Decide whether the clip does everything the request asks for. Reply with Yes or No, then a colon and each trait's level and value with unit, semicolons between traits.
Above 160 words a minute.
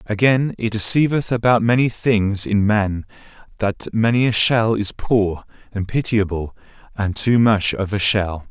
No: average, 155 wpm